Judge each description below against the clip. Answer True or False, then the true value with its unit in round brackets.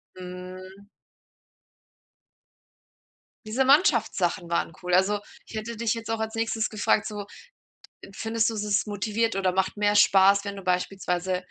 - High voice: True (205 Hz)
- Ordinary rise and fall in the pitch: True (3.0 semitones)